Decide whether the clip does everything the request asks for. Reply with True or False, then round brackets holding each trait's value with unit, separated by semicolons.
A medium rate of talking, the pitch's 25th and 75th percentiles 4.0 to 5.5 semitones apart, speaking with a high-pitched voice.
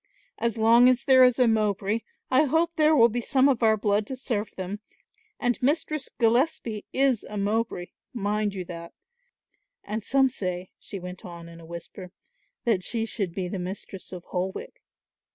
True (175 wpm; 4.9 semitones; 220 Hz)